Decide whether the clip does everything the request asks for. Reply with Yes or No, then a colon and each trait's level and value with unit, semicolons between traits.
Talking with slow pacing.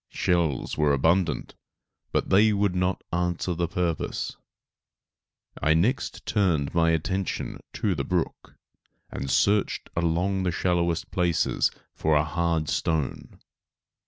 Yes: slow, 120 wpm